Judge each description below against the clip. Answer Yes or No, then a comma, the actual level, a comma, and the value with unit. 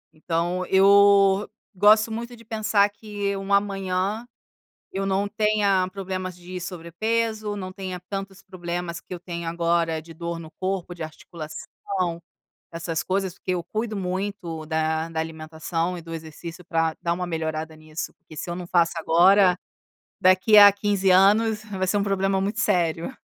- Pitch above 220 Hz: No, medium, 185 Hz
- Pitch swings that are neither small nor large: Yes, average, 3.1 semitones